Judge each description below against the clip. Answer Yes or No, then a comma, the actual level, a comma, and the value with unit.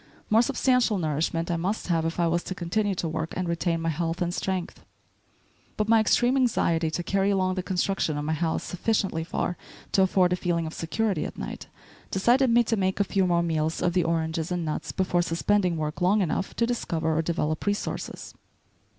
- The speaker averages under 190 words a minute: No, average, 200 wpm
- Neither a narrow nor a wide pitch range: Yes, average, 3.3 semitones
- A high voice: No, medium, 175 Hz